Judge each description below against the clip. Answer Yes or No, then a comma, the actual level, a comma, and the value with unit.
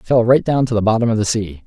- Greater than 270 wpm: Yes, fast, 360 wpm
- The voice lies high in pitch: No, low, 115 Hz